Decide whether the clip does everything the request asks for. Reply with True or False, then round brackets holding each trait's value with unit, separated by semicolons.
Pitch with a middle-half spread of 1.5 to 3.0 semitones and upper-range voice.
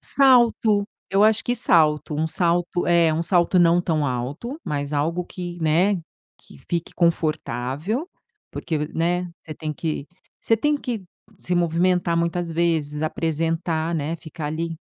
False (2.4 semitones; 170 Hz)